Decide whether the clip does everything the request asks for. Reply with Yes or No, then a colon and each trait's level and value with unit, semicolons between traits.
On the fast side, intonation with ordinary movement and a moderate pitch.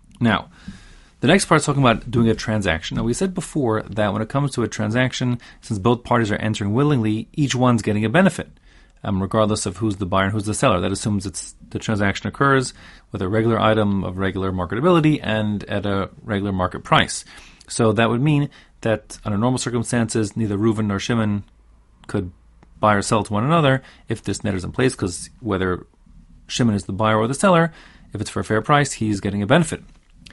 No: fast, 210 wpm; average, 3.7 semitones; low, 110 Hz